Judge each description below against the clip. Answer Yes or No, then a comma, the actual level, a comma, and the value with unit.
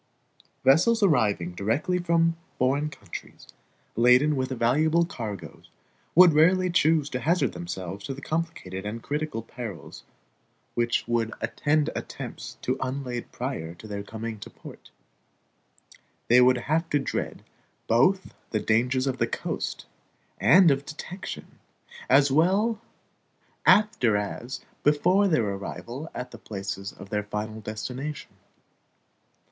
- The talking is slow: Yes, slow, 125 wpm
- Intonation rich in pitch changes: Yes, wide, 6.2 semitones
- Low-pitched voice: Yes, low, 130 Hz